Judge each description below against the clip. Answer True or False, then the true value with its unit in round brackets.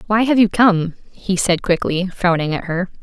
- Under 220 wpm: True (200 wpm)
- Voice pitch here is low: False (190 Hz)